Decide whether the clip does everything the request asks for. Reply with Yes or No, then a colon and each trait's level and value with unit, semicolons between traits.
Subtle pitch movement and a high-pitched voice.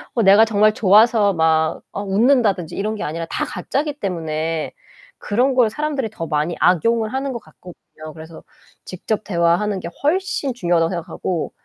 No: wide, 5.5 semitones; high, 200 Hz